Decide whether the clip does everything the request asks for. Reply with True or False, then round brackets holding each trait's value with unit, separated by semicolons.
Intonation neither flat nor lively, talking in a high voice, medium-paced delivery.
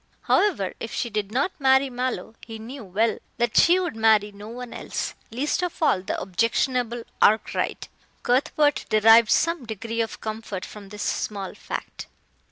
True (3.6 semitones; 230 Hz; 160 wpm)